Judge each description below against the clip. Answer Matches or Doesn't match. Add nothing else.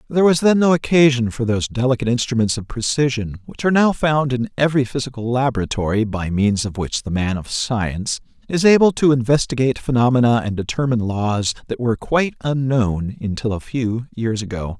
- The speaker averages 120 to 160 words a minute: Doesn't match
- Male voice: Matches